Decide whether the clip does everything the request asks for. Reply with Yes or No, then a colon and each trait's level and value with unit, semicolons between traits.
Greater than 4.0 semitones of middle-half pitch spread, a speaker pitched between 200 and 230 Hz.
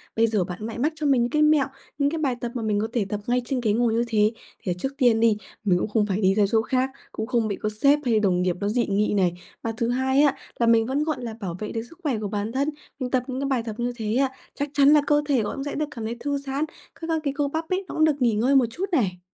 No: average, 4.5 semitones; high, 240 Hz